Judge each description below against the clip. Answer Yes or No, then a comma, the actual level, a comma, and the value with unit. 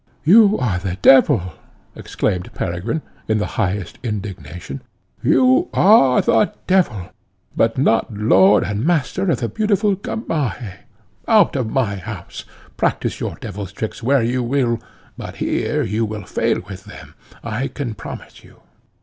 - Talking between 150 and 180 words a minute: No, average, 140 wpm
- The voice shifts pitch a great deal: Yes, wide, 5.8 semitones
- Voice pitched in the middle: No, low, 115 Hz